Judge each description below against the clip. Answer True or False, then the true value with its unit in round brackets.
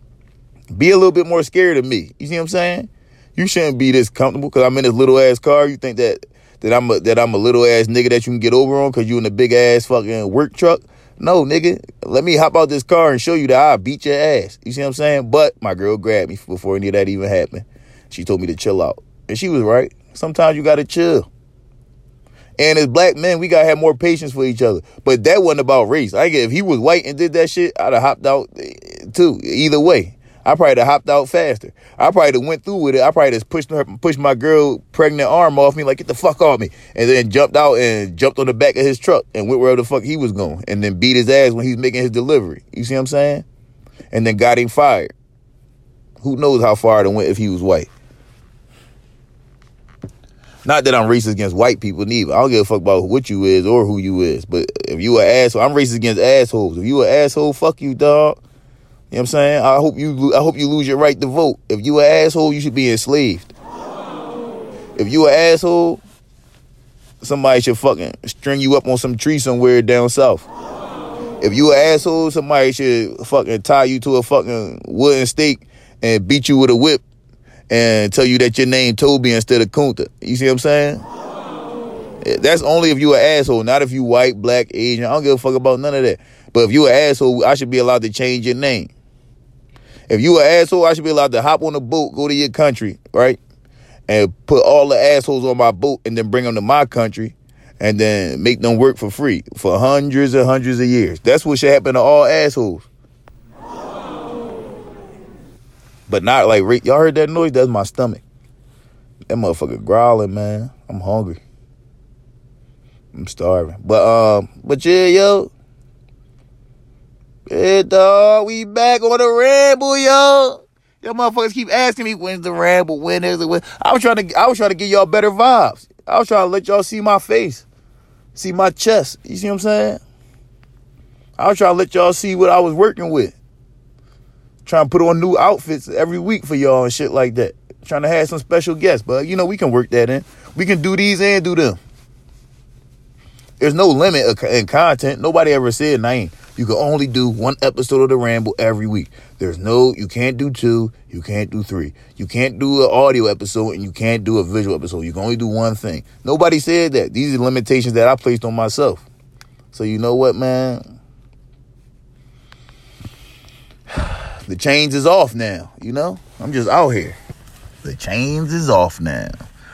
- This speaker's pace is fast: True (220 wpm)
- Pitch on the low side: True (130 Hz)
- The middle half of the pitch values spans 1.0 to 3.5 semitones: False (4.1 semitones)